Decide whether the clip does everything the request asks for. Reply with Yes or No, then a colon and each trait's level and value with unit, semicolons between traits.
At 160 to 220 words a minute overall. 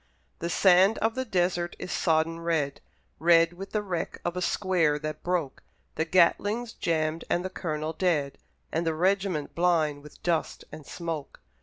Yes: average, 165 wpm